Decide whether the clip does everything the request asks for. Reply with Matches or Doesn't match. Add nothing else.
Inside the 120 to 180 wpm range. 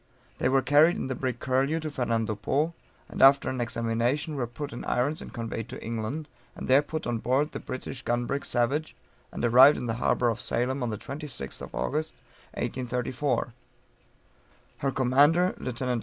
Matches